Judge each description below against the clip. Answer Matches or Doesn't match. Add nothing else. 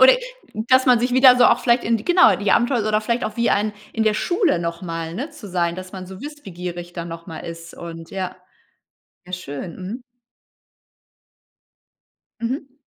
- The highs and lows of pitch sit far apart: Matches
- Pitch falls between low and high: Doesn't match